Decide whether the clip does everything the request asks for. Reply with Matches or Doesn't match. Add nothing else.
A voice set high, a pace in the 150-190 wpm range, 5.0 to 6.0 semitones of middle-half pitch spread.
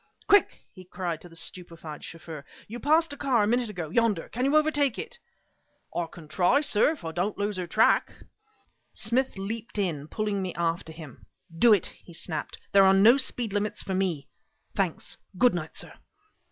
Matches